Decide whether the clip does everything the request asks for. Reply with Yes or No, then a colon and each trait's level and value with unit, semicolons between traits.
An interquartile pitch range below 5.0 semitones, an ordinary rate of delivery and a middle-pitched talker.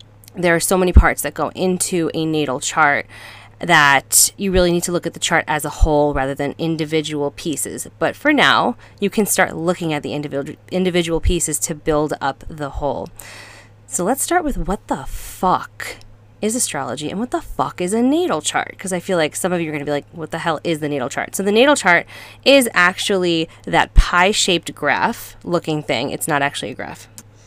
No: average, 4.2 semitones; fast, 210 wpm; medium, 165 Hz